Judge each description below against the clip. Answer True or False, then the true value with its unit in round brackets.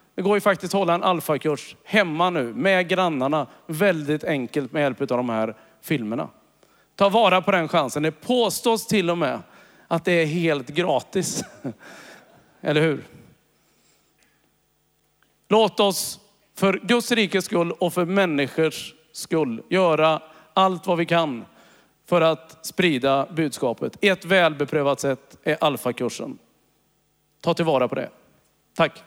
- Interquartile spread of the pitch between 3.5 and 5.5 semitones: True (3.9 semitones)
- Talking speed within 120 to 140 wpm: True (135 wpm)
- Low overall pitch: False (170 Hz)